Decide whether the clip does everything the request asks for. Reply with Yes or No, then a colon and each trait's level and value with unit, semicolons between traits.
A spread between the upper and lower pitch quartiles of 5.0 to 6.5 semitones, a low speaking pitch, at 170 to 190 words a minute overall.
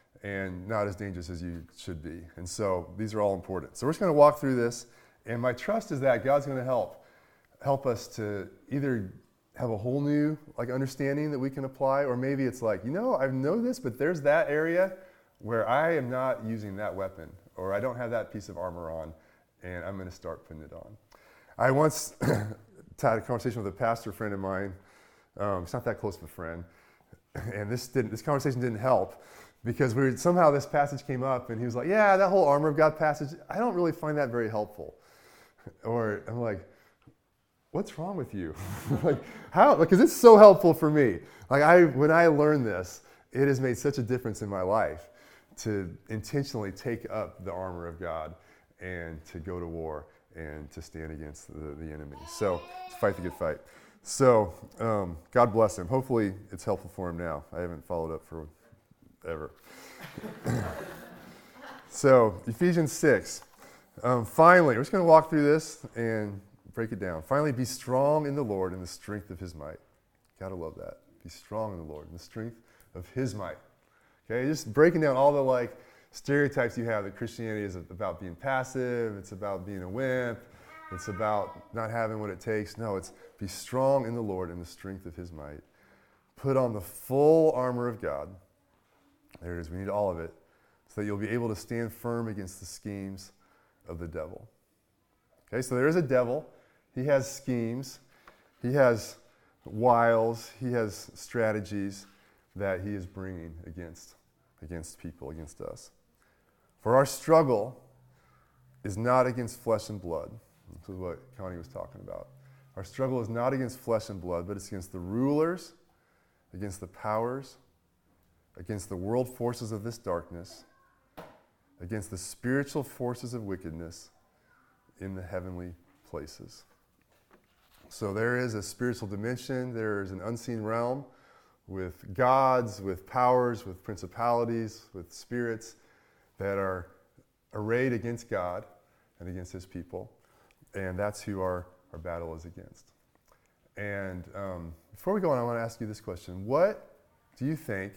Yes: wide, 5.6 semitones; low, 110 Hz; average, 180 wpm